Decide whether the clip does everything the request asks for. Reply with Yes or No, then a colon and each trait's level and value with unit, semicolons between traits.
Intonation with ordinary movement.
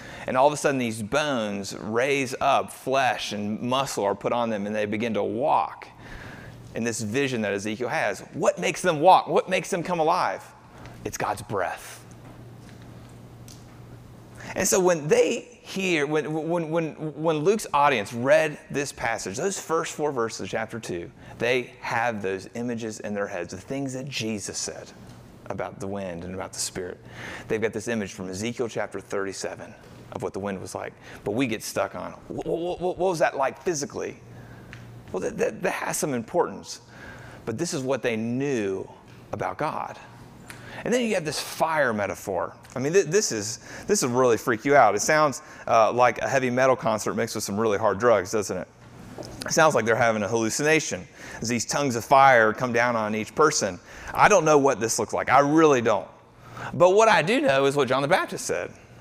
No: wide, 6.3 semitones